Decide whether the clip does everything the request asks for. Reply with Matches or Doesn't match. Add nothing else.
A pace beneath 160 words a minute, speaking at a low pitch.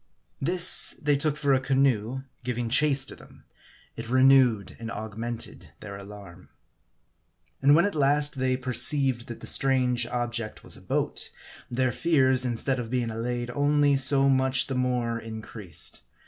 Matches